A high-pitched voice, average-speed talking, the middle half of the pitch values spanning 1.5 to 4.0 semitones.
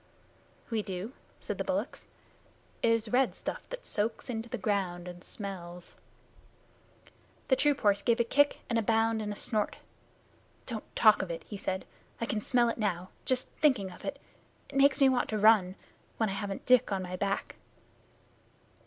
Yes: high, 215 Hz; average, 180 wpm; average, 3.7 semitones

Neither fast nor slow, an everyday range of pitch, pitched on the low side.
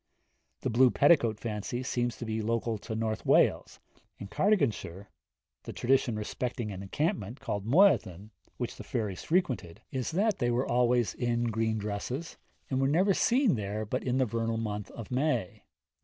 Yes: average, 165 wpm; average, 3.5 semitones; low, 115 Hz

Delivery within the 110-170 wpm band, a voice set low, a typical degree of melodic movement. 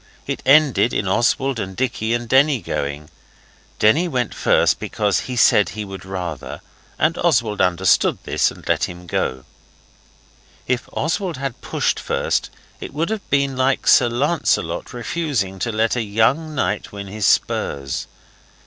No: average, 150 wpm; low, 120 Hz; wide, 5.9 semitones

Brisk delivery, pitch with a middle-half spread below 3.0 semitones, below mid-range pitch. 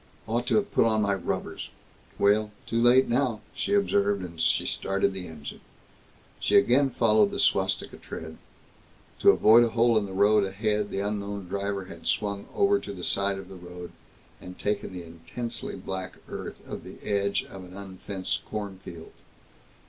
No: average, 175 wpm; narrow, 2.6 semitones; low, 100 Hz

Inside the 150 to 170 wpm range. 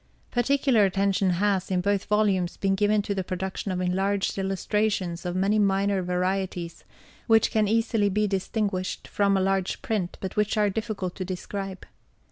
Yes: average, 160 wpm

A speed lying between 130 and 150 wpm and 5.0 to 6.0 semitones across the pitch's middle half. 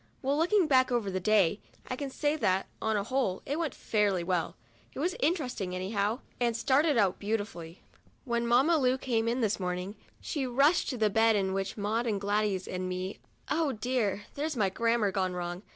No: average, 200 wpm; average, 5.3 semitones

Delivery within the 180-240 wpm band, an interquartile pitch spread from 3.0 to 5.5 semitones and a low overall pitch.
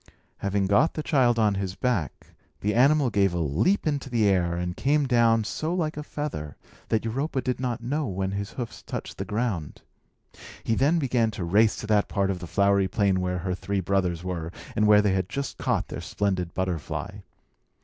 Yes: average, 200 wpm; average, 5.2 semitones; low, 105 Hz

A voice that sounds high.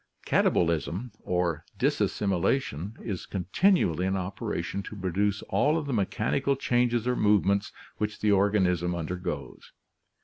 No: low, 100 Hz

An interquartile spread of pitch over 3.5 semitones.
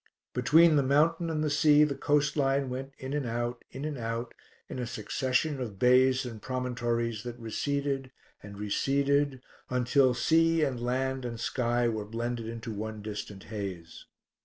No: average, 3.2 semitones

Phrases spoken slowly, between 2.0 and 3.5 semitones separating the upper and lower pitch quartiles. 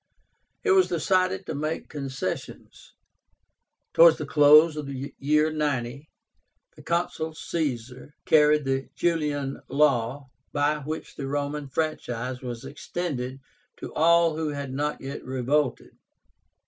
Yes: slow, 120 wpm; narrow, 2.6 semitones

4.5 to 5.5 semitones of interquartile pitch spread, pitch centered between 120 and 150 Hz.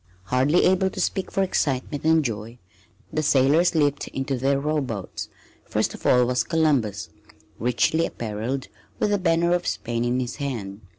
Yes: average, 5.0 semitones; low, 135 Hz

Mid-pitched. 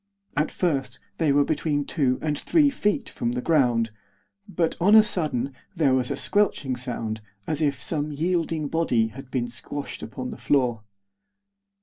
Yes: medium, 145 Hz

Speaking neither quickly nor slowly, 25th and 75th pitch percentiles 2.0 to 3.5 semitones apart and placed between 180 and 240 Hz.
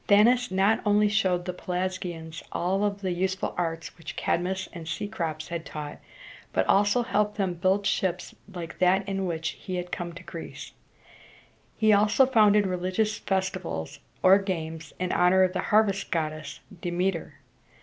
Yes: average, 160 wpm; average, 3.0 semitones; medium, 185 Hz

